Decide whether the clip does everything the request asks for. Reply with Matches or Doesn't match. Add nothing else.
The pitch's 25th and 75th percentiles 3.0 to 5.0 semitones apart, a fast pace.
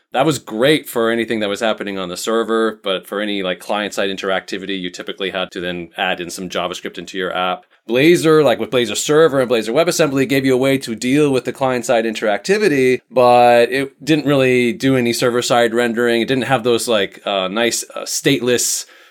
Matches